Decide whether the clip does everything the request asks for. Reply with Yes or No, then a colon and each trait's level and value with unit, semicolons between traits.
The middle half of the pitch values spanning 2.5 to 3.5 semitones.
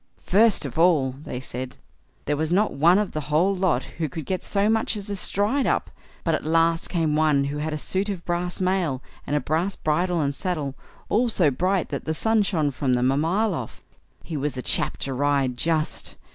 No: average, 4.6 semitones